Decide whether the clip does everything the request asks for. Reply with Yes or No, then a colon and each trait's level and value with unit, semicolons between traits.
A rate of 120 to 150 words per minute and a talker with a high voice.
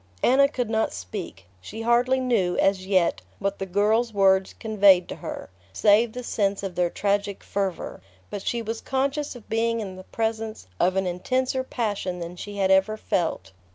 No: average, 180 wpm; high, 205 Hz